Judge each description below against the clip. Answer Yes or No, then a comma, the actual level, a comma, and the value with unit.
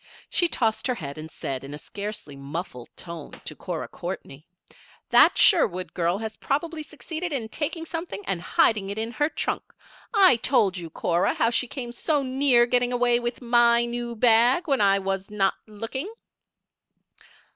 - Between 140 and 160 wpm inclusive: No, average, 170 wpm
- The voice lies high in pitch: Yes, high, 235 Hz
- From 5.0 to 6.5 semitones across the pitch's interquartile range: Yes, wide, 5.5 semitones